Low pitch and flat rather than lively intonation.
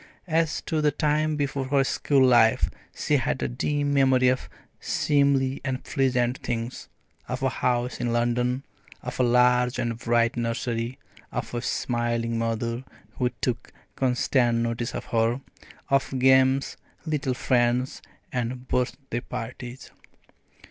Yes: low, 125 Hz; narrow, 2.0 semitones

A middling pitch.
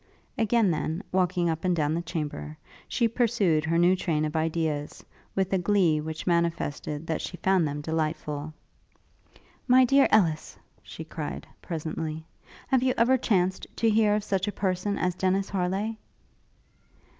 Yes: medium, 180 Hz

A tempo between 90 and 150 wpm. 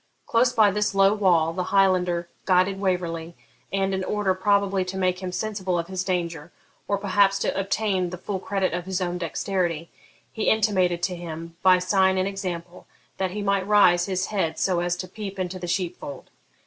No: average, 190 wpm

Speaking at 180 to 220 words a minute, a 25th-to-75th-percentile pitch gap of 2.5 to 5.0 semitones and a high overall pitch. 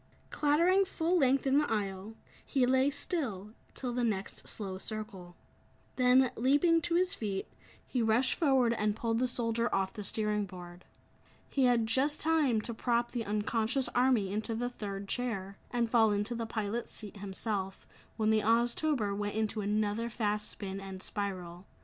No: average, 165 wpm; average, 3.7 semitones; high, 225 Hz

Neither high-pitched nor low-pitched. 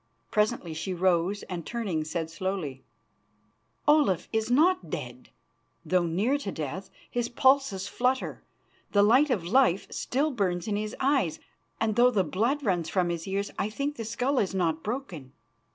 No: high, 205 Hz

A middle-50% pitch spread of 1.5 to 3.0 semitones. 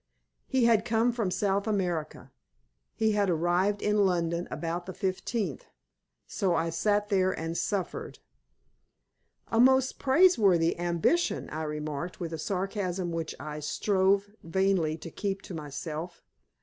No: average, 3.7 semitones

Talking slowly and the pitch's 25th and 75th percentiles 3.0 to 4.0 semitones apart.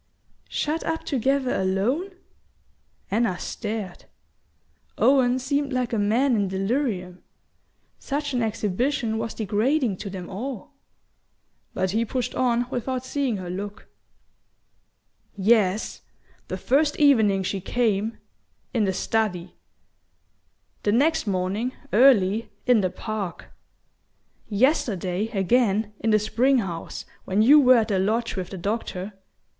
No: slow, 120 wpm; average, 4.7 semitones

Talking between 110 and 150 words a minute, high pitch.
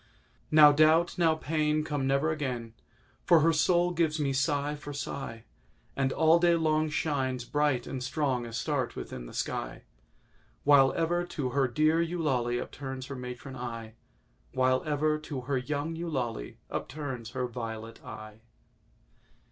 No: average, 140 wpm; medium, 140 Hz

